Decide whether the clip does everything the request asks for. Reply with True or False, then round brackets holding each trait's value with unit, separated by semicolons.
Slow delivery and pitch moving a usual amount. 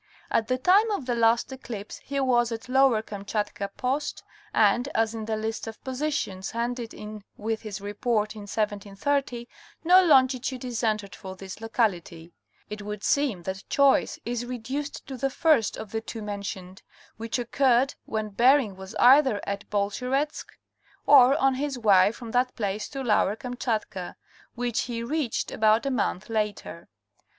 False (160 wpm; 3.7 semitones)